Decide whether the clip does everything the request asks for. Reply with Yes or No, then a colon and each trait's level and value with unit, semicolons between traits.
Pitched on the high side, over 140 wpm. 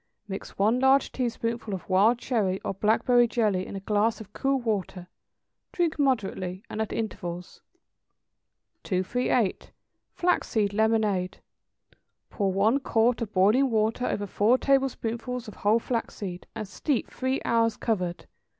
No: high, 220 Hz; slow, 135 wpm